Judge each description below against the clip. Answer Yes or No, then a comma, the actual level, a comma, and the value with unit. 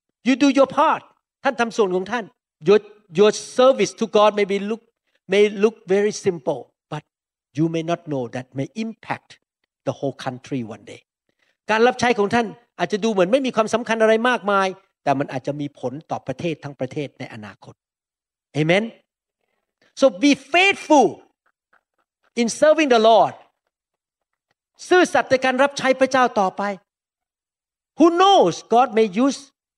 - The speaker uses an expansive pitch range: Yes, wide, 7.7 semitones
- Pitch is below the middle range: No, high, 210 Hz